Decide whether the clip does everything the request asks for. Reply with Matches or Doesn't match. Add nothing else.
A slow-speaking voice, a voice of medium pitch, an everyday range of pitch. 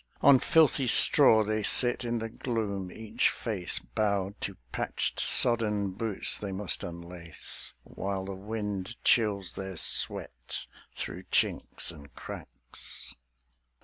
Doesn't match